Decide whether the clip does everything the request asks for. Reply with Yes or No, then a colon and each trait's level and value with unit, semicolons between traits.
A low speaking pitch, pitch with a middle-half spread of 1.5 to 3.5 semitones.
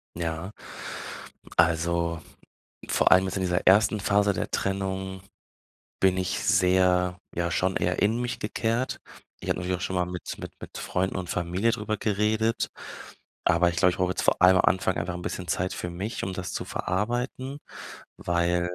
Yes: very low, 95 Hz; narrow, 2.5 semitones